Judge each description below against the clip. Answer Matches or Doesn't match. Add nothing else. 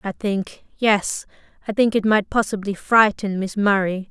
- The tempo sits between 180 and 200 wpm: Doesn't match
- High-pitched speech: Matches